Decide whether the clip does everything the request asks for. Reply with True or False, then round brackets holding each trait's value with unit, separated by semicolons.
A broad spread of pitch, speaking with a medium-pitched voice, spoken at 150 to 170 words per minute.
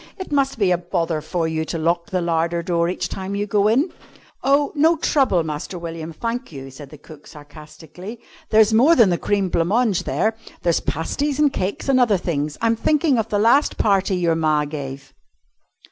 False (6.1 semitones; 180 Hz; 190 wpm)